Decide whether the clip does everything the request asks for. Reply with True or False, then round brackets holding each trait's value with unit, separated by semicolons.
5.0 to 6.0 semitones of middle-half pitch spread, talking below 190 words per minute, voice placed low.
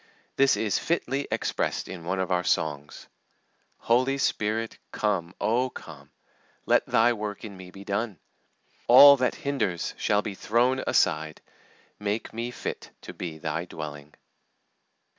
True (5.5 semitones; 140 wpm; 105 Hz)